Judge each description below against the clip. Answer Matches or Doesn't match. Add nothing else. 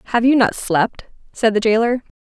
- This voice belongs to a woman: Matches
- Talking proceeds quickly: Doesn't match